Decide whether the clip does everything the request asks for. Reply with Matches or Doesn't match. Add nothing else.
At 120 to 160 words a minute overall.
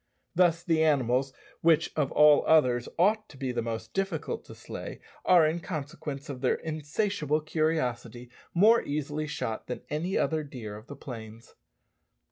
Matches